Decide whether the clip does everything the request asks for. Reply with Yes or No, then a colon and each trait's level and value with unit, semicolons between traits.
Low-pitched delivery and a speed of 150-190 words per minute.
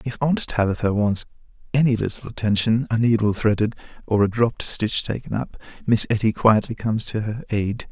Yes: low, 110 Hz; average, 175 wpm